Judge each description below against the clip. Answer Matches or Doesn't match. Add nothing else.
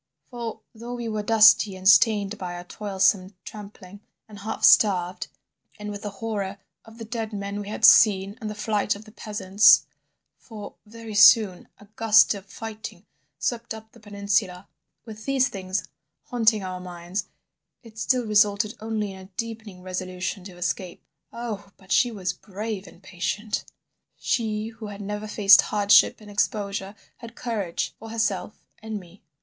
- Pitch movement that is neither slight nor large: Doesn't match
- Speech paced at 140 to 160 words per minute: Matches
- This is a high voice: Matches